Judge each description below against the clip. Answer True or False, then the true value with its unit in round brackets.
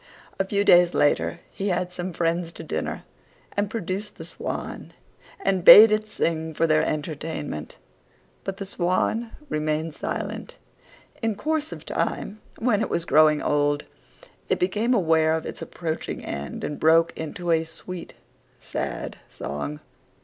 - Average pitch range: True (4.2 semitones)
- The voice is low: False (170 Hz)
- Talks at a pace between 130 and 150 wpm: True (145 wpm)